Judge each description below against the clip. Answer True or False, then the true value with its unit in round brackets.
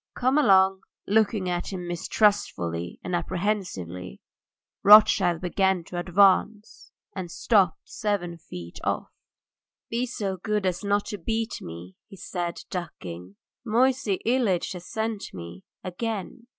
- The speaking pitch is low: False (190 Hz)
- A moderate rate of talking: False (125 wpm)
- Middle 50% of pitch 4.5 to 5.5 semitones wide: False (3.7 semitones)